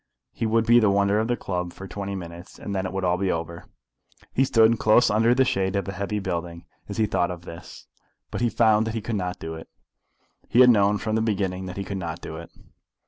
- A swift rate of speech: Yes, fast, 250 wpm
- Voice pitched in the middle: No, low, 100 Hz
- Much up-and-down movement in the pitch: No, average, 3.6 semitones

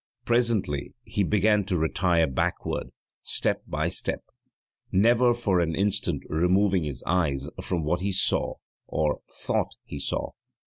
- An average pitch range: Yes, average, 4.5 semitones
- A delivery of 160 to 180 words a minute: No, slow, 135 wpm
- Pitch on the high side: No, very low, 90 Hz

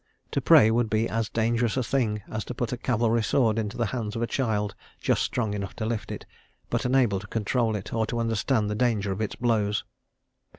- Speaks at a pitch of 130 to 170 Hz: No, low, 110 Hz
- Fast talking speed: Yes, fast, 220 wpm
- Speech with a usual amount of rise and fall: No, narrow, 2.2 semitones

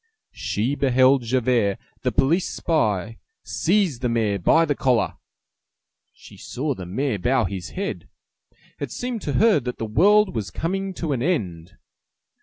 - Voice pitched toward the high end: No, low, 130 Hz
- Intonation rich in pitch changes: Yes, wide, 7.4 semitones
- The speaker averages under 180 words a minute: Yes, average, 150 wpm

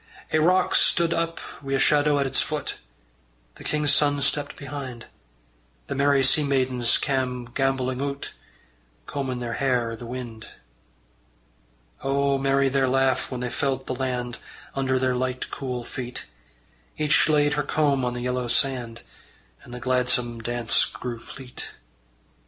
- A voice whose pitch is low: Yes, low, 130 Hz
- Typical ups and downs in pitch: No, narrow, 2.1 semitones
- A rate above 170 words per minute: No, average, 150 wpm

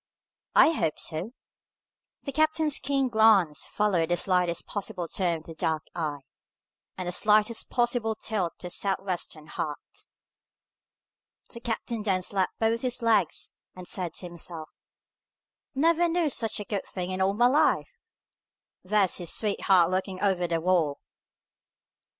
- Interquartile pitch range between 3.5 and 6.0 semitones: Yes, average, 4.6 semitones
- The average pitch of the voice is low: No, high, 195 Hz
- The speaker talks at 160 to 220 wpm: No, average, 145 wpm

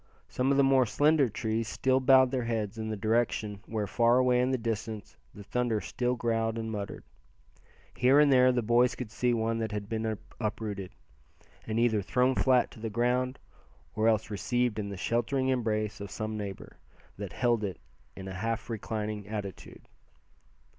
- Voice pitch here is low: Yes, low, 115 Hz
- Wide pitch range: No, narrow, 2.6 semitones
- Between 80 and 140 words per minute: No, average, 180 wpm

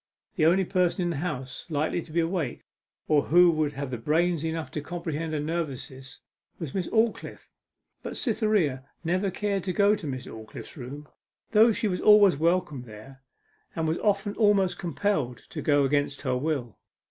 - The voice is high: No, medium, 160 Hz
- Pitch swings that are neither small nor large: Yes, average, 4.6 semitones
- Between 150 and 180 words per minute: Yes, average, 170 wpm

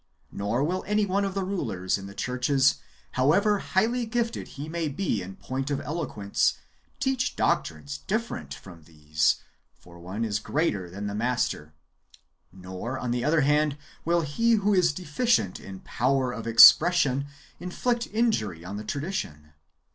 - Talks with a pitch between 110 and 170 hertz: Yes, low, 135 Hz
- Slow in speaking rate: No, average, 155 wpm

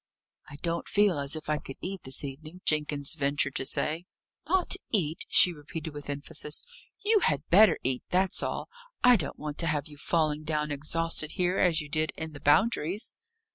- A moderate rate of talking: Yes, average, 185 wpm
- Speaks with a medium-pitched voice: Yes, medium, 155 Hz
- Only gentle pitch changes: No, average, 3.3 semitones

